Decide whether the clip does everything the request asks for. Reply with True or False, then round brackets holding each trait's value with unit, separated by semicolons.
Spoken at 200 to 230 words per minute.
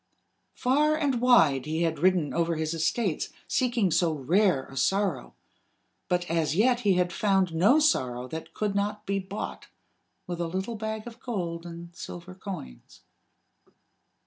False (150 wpm)